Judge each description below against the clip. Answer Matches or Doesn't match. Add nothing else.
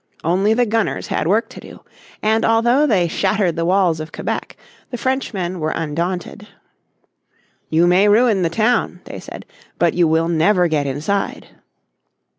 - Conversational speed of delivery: Matches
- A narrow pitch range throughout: Doesn't match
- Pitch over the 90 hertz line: Matches